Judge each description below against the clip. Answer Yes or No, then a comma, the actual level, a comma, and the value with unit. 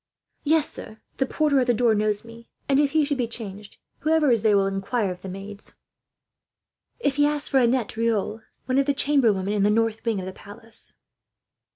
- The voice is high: Yes, high, 230 Hz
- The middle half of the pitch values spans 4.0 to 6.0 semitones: Yes, average, 5.0 semitones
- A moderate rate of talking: No, fast, 210 wpm